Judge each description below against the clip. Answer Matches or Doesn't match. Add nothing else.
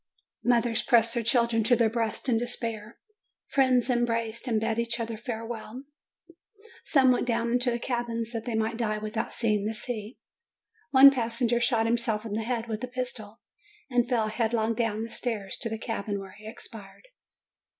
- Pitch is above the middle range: Matches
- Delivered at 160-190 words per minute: Matches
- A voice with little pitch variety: Matches